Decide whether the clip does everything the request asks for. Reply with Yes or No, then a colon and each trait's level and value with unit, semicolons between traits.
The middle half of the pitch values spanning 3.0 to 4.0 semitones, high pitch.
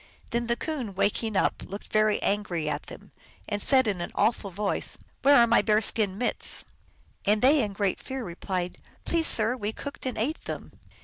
Yes: average, 3.6 semitones; high, 215 Hz